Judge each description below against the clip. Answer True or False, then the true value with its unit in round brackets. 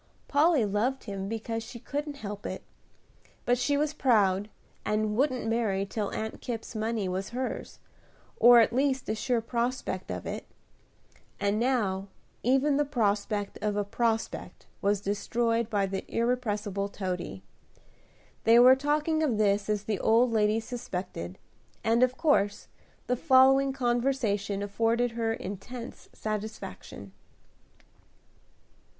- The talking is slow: True (130 wpm)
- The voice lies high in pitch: True (225 Hz)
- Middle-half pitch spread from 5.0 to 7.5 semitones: False (3.6 semitones)